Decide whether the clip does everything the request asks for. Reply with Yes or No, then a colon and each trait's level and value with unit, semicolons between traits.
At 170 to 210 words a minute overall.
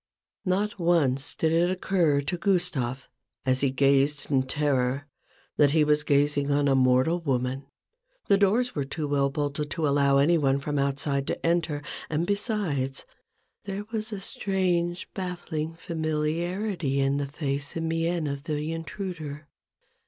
No: average, 150 wpm